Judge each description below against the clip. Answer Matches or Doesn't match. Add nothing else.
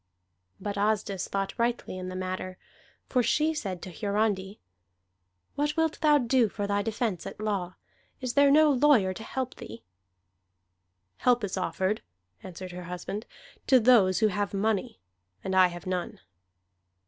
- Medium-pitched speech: Doesn't match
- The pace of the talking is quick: Doesn't match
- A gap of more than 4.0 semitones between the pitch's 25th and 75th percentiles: Matches